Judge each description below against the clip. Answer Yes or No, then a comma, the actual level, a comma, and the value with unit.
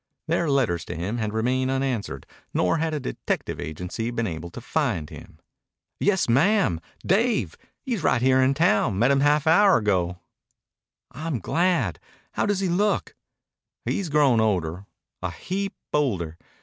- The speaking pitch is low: Yes, low, 130 Hz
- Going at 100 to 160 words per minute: Yes, average, 155 wpm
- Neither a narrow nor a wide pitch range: No, wide, 8.2 semitones